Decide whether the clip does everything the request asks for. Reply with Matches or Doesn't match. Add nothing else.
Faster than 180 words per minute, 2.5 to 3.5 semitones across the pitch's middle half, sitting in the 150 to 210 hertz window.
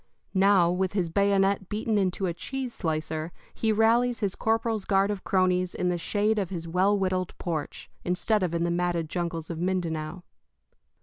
Doesn't match